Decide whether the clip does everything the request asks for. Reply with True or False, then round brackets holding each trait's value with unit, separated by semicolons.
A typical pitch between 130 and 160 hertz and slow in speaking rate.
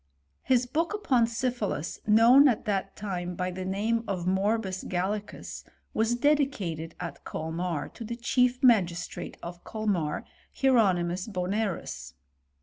False (205 Hz; 125 wpm)